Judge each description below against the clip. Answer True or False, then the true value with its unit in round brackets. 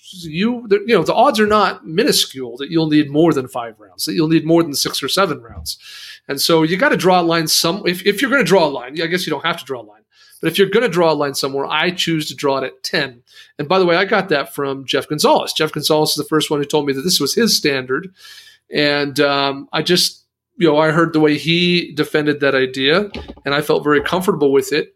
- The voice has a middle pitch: True (155 Hz)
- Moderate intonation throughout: True (4.1 semitones)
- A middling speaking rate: False (265 wpm)